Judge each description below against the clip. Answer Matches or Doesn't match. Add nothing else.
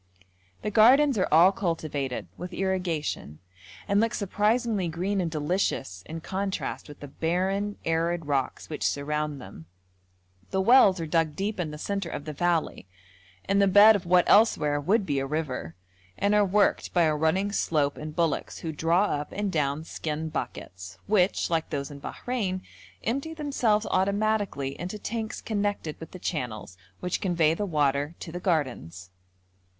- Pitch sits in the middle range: Matches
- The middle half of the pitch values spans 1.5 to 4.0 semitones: Doesn't match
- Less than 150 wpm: Doesn't match